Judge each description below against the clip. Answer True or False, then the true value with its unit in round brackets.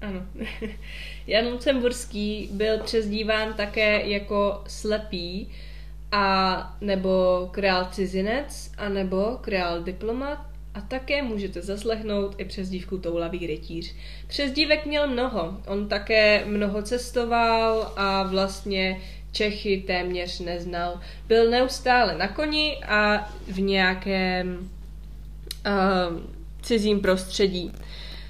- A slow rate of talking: True (95 wpm)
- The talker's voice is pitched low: False (200 Hz)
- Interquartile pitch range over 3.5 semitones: False (2.9 semitones)